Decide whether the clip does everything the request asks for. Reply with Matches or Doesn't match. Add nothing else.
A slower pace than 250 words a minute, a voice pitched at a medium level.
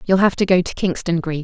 Doesn't match